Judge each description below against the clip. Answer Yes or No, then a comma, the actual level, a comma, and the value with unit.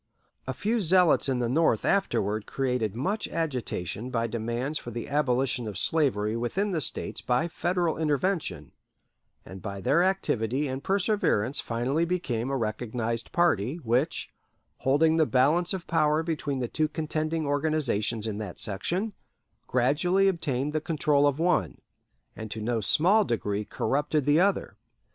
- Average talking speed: Yes, average, 150 wpm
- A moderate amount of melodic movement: No, wide, 5.8 semitones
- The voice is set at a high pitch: No, medium, 140 Hz